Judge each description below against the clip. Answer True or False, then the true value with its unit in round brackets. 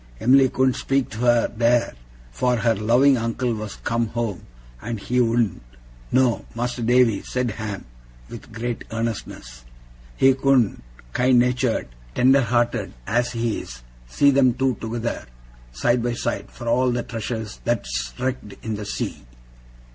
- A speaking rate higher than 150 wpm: False (145 wpm)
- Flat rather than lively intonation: True (1.9 semitones)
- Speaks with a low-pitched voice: True (120 Hz)